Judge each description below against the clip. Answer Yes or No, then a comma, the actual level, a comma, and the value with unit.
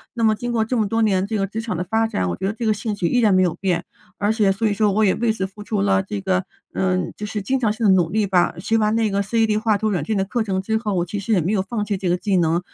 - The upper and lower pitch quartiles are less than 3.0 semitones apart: Yes, narrow, 2.6 semitones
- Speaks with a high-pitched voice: Yes, high, 205 Hz